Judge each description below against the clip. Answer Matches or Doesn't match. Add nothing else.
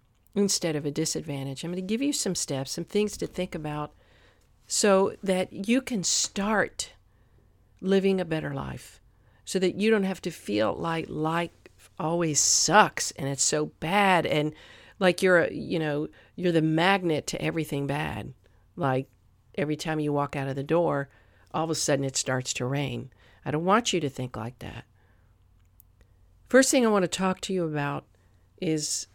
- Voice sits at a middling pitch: Matches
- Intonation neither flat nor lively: Doesn't match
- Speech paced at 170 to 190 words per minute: Matches